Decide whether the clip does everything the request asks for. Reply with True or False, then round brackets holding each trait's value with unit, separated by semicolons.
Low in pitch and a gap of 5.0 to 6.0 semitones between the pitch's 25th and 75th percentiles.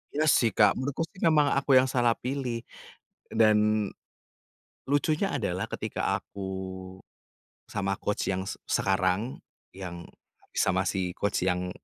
True (110 Hz; 5.6 semitones)